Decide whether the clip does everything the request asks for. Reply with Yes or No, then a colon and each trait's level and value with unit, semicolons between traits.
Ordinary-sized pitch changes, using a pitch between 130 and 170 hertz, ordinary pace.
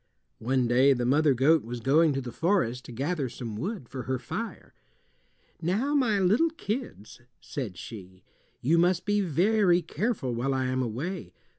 No: wide, 7.2 semitones; medium, 140 Hz; average, 165 wpm